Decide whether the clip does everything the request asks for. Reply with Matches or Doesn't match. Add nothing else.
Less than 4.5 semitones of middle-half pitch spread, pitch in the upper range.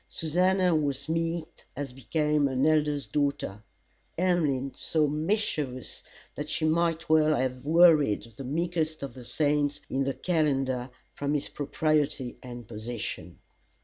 Doesn't match